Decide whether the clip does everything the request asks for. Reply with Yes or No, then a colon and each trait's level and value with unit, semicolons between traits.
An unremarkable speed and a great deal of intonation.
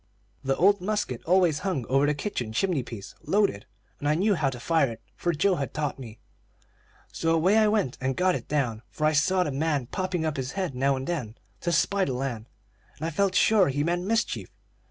No: fast, 215 wpm; wide, 5.7 semitones